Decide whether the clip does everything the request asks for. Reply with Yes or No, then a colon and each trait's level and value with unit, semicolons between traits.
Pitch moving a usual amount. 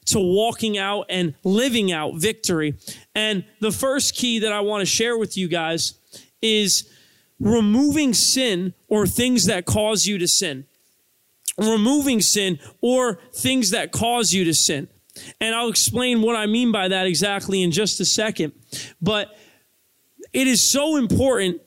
Yes: average, 4.2 semitones